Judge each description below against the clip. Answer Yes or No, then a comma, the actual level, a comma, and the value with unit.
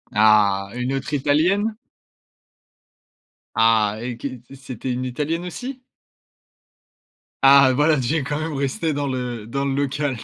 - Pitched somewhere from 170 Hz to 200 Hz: No, low, 135 Hz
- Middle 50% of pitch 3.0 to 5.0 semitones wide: Yes, average, 3.4 semitones